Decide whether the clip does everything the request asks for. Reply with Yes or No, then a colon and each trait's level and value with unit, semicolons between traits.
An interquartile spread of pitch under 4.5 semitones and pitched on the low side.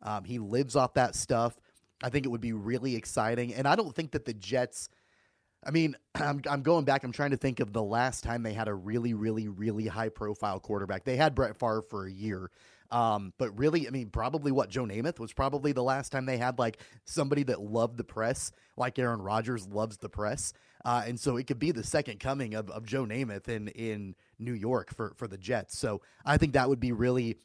Yes: average, 3.4 semitones; low, 120 Hz